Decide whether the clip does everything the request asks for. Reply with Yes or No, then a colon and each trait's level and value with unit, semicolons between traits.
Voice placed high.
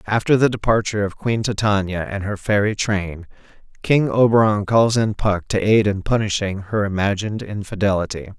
No: low, 105 Hz